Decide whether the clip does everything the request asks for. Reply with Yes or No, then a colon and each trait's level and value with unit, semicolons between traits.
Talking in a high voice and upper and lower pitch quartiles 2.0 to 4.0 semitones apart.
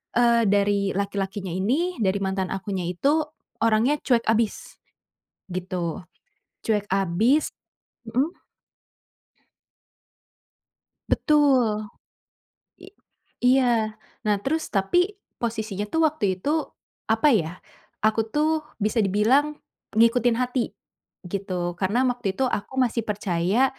No: high, 220 Hz; average, 4.7 semitones